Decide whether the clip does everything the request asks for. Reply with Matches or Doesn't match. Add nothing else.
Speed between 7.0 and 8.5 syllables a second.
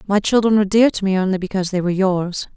Matches